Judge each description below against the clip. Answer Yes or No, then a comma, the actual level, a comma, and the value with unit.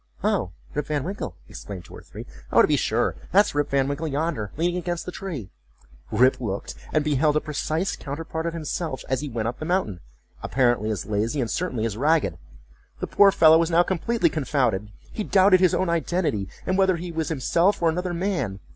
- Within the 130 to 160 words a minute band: No, average, 200 wpm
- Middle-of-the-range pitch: Yes, medium, 155 Hz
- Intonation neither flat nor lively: No, wide, 6.3 semitones